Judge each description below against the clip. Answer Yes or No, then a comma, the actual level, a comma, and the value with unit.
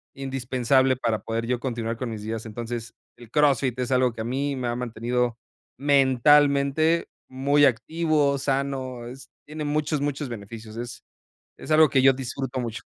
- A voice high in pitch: No, low, 130 Hz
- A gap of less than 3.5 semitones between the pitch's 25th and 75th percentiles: Yes, average, 2.9 semitones